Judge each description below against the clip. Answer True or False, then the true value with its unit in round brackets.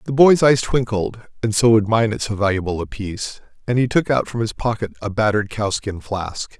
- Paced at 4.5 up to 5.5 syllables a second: True (5.4 syllables/s)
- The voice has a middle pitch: False (110 Hz)